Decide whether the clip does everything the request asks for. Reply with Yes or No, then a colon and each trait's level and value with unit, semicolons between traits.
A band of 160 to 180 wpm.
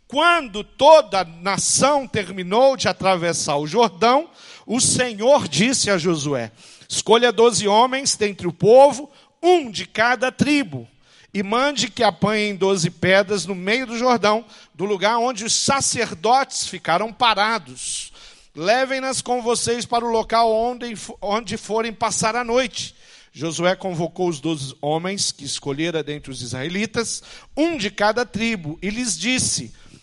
No: average, 140 wpm